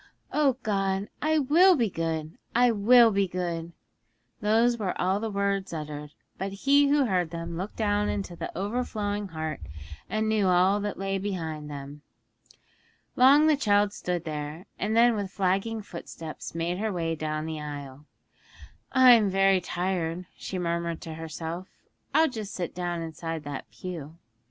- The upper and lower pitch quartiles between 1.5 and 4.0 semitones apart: No, average, 4.5 semitones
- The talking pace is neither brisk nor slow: Yes, average, 155 wpm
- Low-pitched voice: No, high, 190 Hz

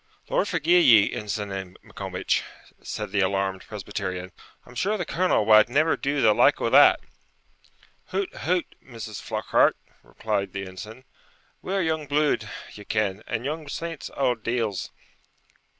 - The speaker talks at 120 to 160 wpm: Yes, average, 140 wpm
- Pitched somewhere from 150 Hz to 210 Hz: No, low, 115 Hz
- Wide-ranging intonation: Yes, wide, 7.4 semitones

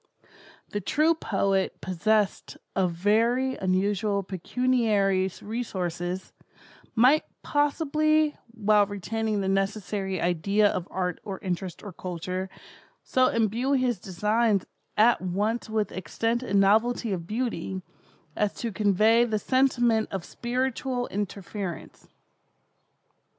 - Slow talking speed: Yes, slow, 110 wpm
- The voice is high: Yes, high, 210 Hz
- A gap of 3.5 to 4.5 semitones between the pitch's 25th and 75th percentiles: Yes, average, 3.9 semitones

